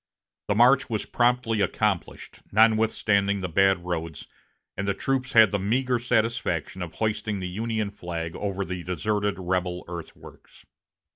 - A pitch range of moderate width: Yes, average, 3.5 semitones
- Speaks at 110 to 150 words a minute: Yes, average, 140 wpm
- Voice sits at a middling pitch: No, low, 100 Hz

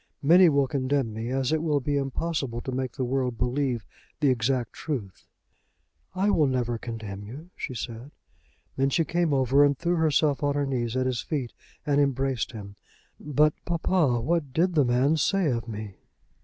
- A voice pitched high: No, low, 135 Hz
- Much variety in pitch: No, average, 3.7 semitones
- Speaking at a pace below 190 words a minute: Yes, average, 180 wpm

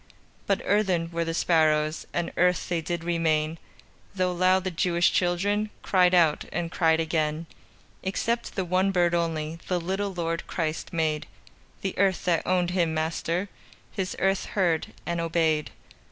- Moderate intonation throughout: No, narrow, 2.2 semitones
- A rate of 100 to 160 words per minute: Yes, average, 155 wpm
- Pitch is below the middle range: No, medium, 170 Hz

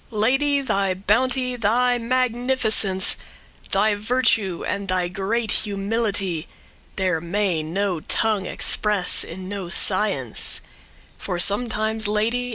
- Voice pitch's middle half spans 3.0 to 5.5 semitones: Yes, average, 3.7 semitones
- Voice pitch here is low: No, high, 210 Hz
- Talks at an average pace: No, slow, 105 wpm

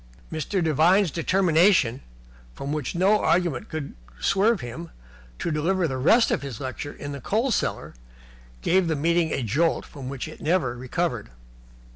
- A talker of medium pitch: Yes, medium, 160 Hz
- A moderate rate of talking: Yes, average, 155 wpm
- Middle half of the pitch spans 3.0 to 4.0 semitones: No, average, 5.0 semitones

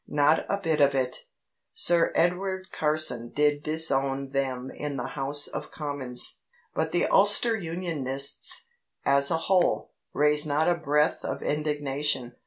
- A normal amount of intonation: Yes, average, 3.0 semitones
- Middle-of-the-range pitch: Yes, medium, 150 Hz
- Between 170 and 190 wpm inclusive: No, average, 140 wpm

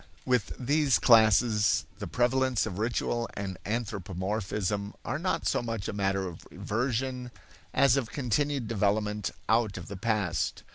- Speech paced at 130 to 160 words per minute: Yes, average, 140 wpm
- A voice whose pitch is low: Yes, low, 110 Hz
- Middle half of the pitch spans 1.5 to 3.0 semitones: No, average, 3.5 semitones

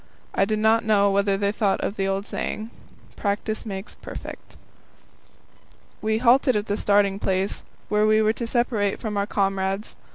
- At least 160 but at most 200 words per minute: Yes, average, 165 wpm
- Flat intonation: Yes, narrow, 1.7 semitones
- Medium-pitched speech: No, high, 205 Hz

